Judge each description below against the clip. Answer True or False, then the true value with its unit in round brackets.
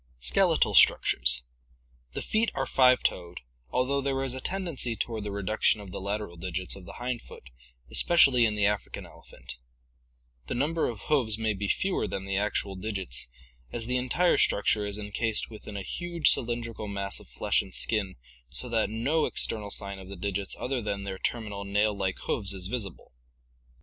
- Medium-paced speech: True (180 wpm)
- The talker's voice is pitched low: True (105 Hz)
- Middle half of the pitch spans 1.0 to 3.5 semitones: False (4.1 semitones)